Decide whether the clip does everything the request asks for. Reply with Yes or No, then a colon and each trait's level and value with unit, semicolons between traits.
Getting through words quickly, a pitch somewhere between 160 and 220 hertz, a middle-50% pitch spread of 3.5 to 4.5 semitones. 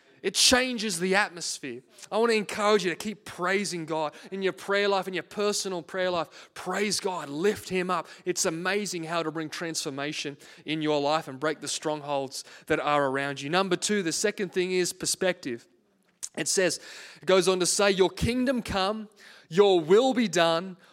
No: average, 185 wpm; medium, 185 Hz; average, 4.2 semitones